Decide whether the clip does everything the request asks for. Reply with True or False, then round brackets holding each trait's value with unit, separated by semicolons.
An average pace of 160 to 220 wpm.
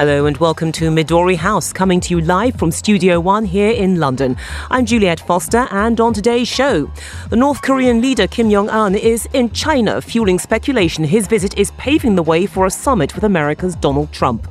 True (200 wpm)